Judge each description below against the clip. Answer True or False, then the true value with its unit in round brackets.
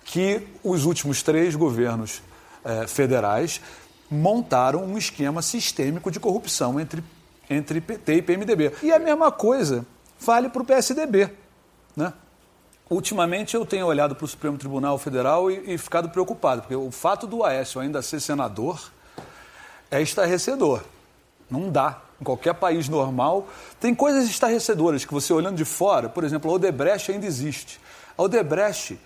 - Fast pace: False (150 wpm)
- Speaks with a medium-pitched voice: True (170 Hz)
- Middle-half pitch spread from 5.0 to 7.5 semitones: True (5.5 semitones)